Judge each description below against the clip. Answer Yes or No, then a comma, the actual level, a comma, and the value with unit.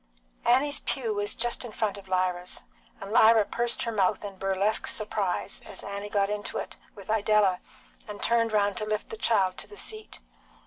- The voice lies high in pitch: Yes, high, 210 Hz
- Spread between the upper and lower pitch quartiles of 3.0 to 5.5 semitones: No, narrow, 2.6 semitones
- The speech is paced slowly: No, average, 185 wpm